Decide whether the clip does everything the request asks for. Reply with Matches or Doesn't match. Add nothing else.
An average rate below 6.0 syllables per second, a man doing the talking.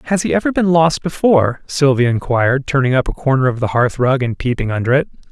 Doesn't match